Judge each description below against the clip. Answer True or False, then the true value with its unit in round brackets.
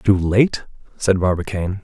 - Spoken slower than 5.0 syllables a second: True (4.7 syllables/s)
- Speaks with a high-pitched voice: False (95 Hz)